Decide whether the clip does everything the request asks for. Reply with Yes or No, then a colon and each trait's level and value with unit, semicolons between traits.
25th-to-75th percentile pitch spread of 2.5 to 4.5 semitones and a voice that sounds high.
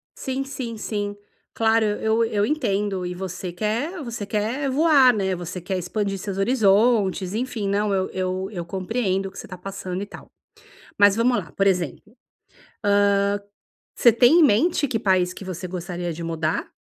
Yes: average, 3.6 semitones; high, 205 Hz